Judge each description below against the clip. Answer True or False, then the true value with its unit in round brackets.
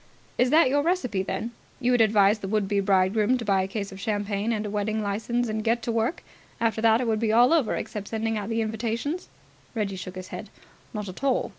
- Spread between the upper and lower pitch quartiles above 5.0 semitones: False (2.6 semitones)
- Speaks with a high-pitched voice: True (220 Hz)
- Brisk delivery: True (235 wpm)